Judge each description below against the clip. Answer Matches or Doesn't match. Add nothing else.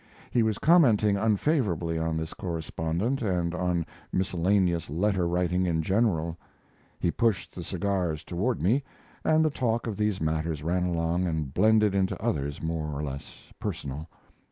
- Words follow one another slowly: Doesn't match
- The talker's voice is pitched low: Matches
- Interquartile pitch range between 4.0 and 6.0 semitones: Matches